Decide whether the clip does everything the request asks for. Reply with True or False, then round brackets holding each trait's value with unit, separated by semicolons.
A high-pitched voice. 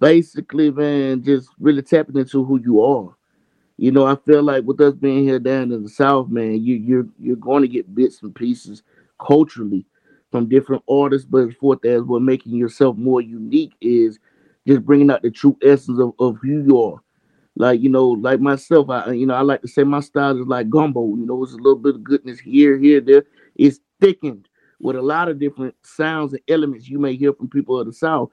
False (135 Hz)